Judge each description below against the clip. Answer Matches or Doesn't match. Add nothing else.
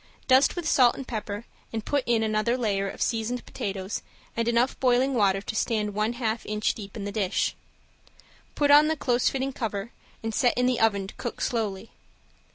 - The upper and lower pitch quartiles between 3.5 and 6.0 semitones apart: Doesn't match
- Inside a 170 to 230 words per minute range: Matches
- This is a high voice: Matches